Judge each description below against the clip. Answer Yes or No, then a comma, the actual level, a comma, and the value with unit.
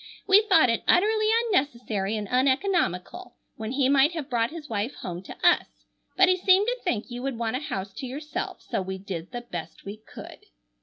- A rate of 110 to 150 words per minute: No, average, 200 wpm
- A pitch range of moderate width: No, wide, 8.4 semitones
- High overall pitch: Yes, very high, 255 Hz